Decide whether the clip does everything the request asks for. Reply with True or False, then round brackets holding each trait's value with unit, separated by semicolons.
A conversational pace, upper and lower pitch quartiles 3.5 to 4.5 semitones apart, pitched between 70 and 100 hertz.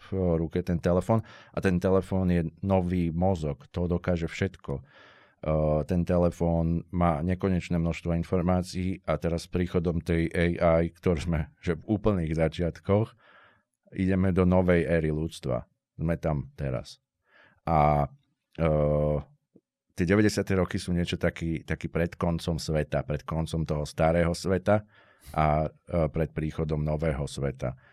False (135 wpm; 2.6 semitones; 85 Hz)